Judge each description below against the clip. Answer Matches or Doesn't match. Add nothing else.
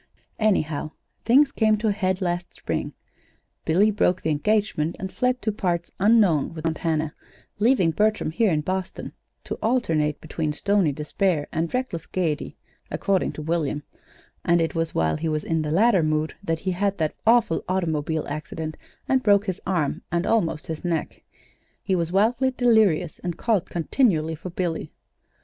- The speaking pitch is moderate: Matches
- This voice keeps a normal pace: Matches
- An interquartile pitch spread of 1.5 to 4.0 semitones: Doesn't match